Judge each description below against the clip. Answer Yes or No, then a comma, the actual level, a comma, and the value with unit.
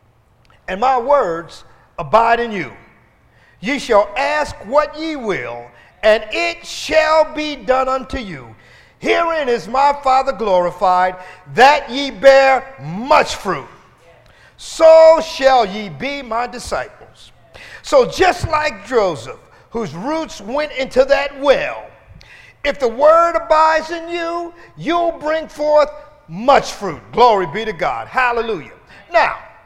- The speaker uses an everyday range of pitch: No, wide, 7.0 semitones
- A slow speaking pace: Yes, slow, 125 wpm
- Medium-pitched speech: No, very high, 265 Hz